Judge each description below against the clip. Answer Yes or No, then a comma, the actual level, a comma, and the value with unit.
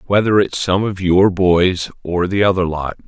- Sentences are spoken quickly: No, average, 195 wpm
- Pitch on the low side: Yes, very low, 95 Hz